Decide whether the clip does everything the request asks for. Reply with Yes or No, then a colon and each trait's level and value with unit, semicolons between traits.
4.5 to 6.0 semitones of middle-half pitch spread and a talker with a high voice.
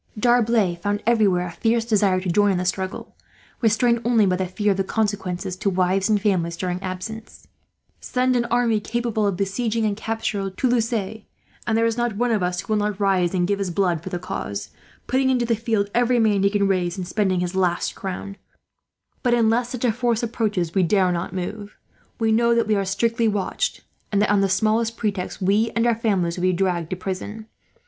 No: average, 3.5 semitones; high, 205 Hz